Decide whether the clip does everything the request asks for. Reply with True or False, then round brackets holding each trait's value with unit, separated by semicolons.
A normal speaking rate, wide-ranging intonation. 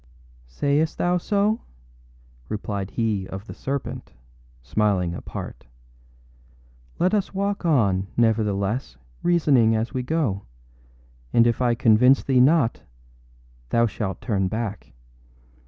False (115 wpm; 6.1 semitones)